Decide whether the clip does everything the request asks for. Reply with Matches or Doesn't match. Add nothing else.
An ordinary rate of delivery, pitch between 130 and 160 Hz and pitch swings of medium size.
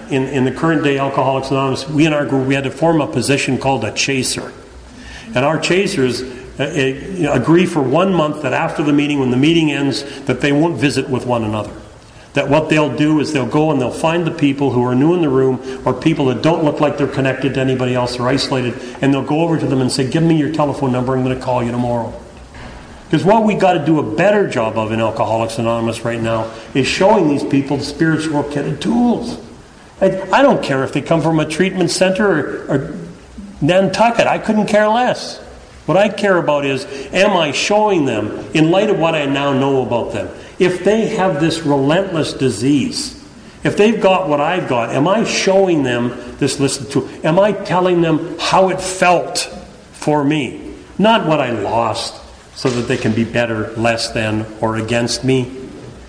Doesn't match